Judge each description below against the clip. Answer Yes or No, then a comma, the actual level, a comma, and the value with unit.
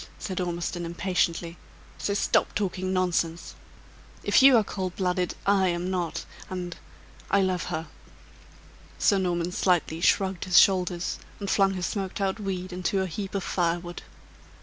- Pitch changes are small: Yes, narrow, 1.7 semitones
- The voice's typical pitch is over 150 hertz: Yes, medium, 185 Hz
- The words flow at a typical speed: Yes, average, 150 wpm